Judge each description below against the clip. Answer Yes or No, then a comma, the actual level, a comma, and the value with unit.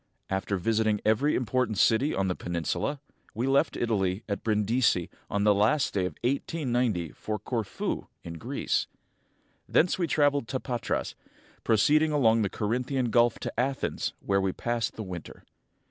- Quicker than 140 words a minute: Yes, average, 160 wpm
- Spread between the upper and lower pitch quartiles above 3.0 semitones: Yes, average, 4.4 semitones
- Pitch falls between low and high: No, low, 115 Hz